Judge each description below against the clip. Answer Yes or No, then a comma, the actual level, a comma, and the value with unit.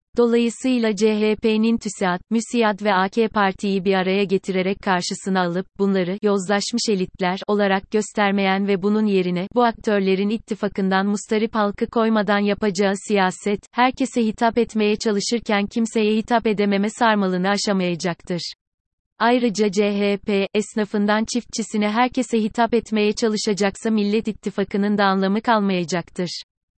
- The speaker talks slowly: No, average, 110 wpm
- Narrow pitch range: Yes, narrow, 2.3 semitones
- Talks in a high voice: Yes, high, 210 Hz